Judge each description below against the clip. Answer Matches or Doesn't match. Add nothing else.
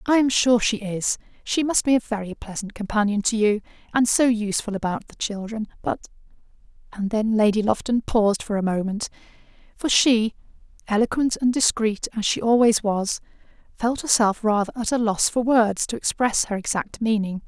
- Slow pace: Doesn't match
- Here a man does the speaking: Doesn't match